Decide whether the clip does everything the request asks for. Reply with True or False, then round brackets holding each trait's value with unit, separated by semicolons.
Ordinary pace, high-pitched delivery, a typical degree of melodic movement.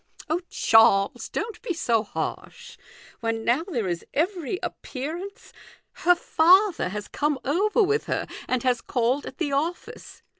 False (150 wpm; 295 Hz; 7.4 semitones)